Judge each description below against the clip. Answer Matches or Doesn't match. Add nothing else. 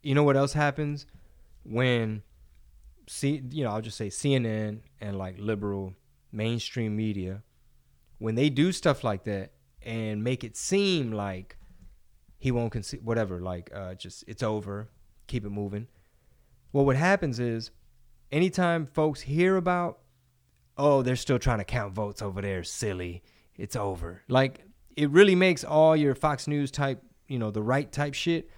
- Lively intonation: Matches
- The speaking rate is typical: Matches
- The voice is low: Matches